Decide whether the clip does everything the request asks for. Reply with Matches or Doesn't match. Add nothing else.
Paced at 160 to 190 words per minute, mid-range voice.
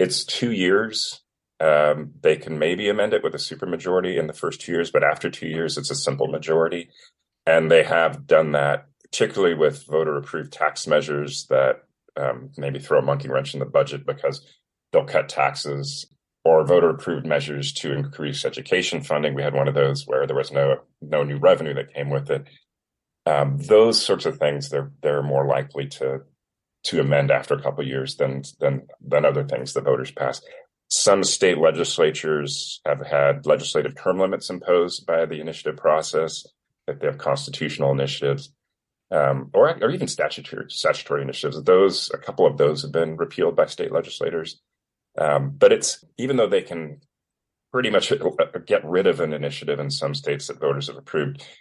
Doesn't match